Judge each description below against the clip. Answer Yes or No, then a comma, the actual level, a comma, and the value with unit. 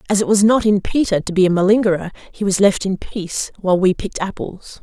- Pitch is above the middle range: Yes, high, 195 Hz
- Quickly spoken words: Yes, fast, 235 wpm